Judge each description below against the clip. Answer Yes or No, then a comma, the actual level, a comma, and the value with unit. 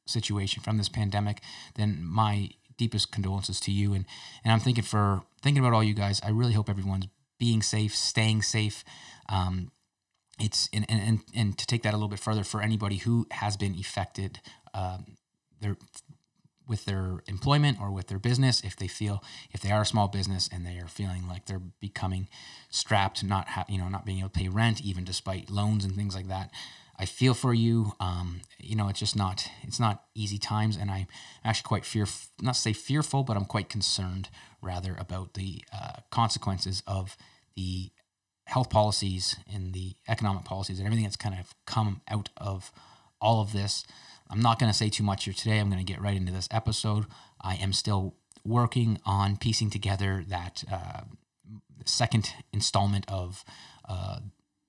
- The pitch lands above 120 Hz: No, low, 105 Hz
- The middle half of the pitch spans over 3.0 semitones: No, narrow, 2.6 semitones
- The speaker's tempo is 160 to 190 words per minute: Yes, average, 185 wpm